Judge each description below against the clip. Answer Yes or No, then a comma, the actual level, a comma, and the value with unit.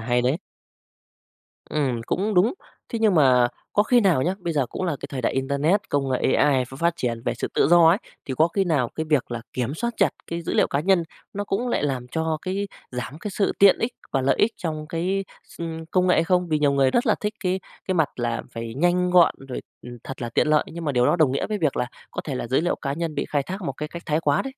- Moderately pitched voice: Yes, medium, 160 Hz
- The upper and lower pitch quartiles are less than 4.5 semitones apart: No, average, 5.3 semitones